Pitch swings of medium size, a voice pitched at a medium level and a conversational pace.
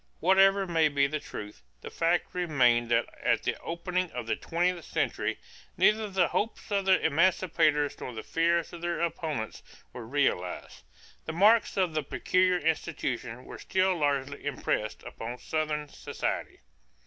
Yes: average, 4.5 semitones; medium, 160 Hz; average, 150 wpm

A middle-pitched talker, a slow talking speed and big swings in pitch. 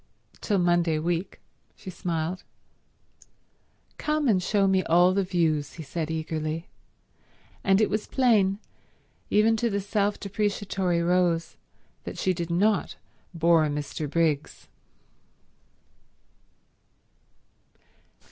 No: medium, 180 Hz; slow, 105 wpm; average, 3.5 semitones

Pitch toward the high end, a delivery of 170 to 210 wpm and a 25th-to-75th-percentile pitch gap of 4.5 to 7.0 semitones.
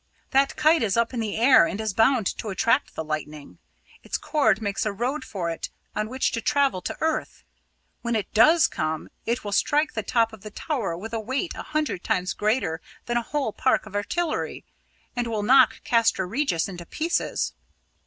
Yes: high, 225 Hz; average, 195 wpm; average, 5.0 semitones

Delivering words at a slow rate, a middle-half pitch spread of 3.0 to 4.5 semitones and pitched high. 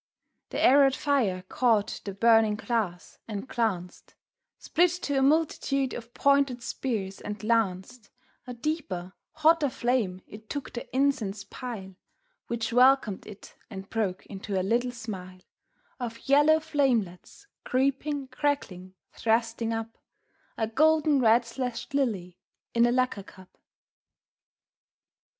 No: slow, 125 wpm; average, 5.1 semitones; high, 235 Hz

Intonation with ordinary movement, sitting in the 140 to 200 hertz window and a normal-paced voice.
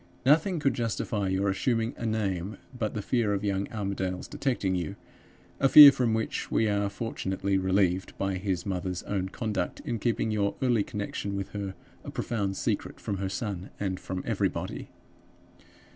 No: average, 3.0 semitones; low, 100 Hz; average, 165 wpm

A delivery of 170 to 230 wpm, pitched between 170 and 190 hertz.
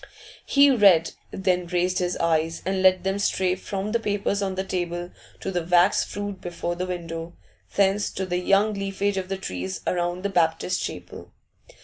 Yes: average, 175 wpm; medium, 185 Hz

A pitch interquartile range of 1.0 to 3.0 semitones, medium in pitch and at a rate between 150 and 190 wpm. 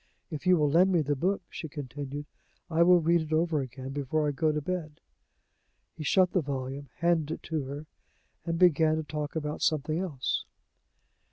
Yes: average, 2.7 semitones; medium, 155 Hz; average, 185 wpm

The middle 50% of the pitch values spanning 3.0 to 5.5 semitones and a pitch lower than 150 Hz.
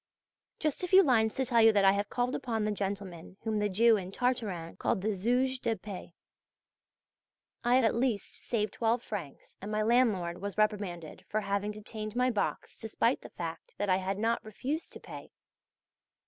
No: average, 3.3 semitones; high, 215 Hz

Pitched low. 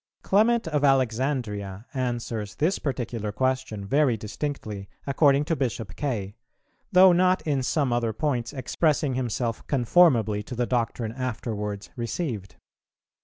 Yes: low, 125 Hz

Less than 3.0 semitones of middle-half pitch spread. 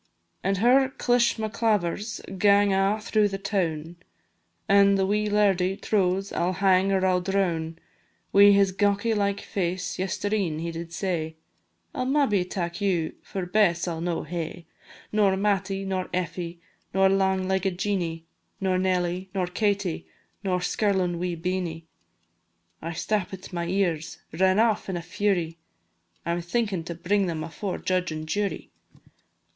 Yes: narrow, 2.6 semitones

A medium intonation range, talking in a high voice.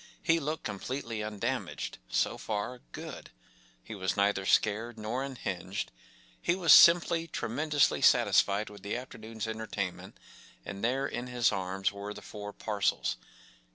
No: average, 4.2 semitones; low, 110 Hz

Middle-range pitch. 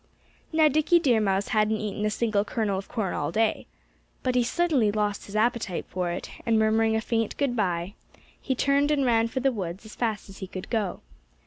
No: high, 220 Hz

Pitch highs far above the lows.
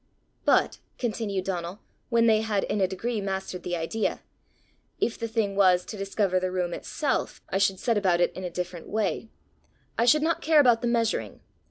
No: average, 3.8 semitones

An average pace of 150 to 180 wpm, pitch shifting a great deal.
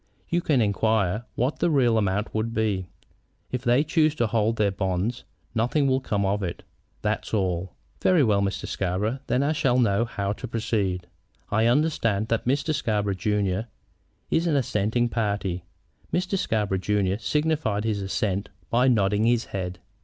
No: average, 165 wpm; average, 4.1 semitones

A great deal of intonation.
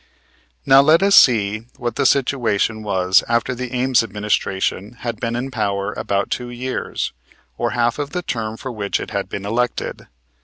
No: average, 3.5 semitones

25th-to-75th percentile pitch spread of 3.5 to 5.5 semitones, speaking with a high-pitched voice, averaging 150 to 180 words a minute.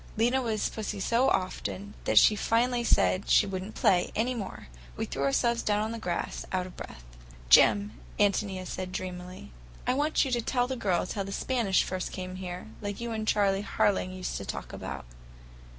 No: average, 3.8 semitones; high, 205 Hz; average, 200 wpm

